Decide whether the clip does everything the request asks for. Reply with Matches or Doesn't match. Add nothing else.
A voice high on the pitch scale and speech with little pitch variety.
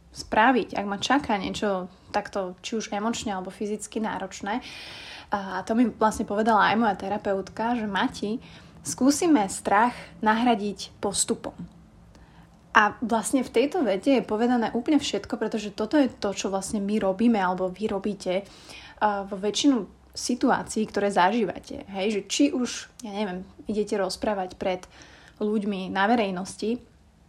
Doesn't match